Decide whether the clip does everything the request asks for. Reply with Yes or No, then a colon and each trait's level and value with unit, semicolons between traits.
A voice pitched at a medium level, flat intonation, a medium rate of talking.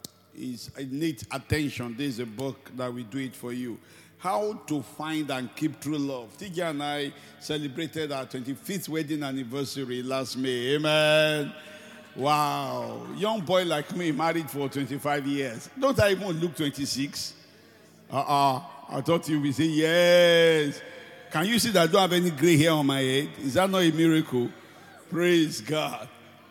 No: medium, 150 Hz; average, 3.4 semitones; average, 165 wpm